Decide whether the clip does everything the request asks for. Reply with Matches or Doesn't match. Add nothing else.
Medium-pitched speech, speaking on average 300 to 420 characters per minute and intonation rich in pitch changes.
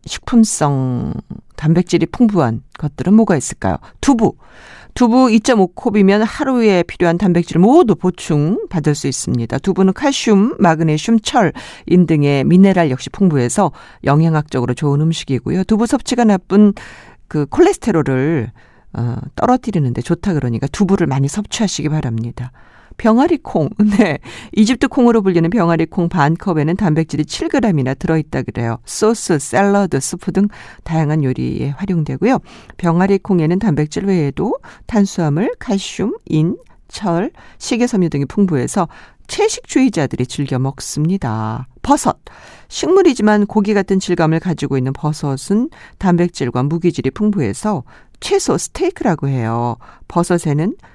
Matches